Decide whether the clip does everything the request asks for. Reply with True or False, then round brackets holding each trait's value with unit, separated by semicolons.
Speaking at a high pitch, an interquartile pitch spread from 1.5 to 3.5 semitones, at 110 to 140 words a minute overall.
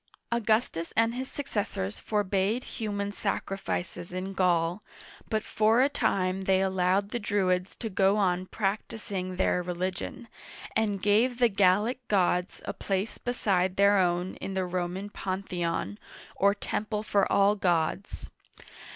True (195 Hz; 2.5 semitones; 135 wpm)